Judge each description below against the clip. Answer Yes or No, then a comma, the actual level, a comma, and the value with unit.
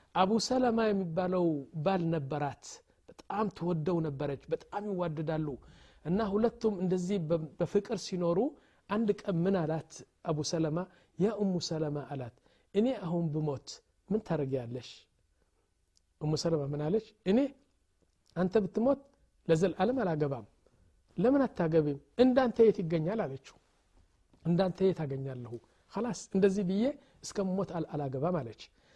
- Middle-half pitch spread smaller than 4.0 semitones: No, wide, 5.6 semitones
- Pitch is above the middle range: No, medium, 175 Hz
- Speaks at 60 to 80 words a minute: No, average, 105 wpm